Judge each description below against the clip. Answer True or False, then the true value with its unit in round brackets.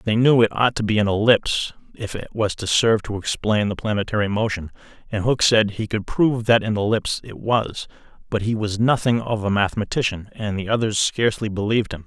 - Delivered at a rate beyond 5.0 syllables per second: True (5.9 syllables/s)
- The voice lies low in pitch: True (110 Hz)